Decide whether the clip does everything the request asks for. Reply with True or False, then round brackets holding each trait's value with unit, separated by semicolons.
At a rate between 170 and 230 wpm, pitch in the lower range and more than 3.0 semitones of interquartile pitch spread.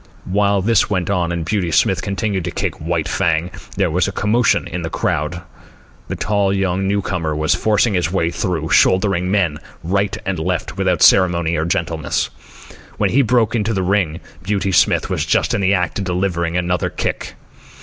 False (185 wpm; 90 Hz; 2.7 semitones)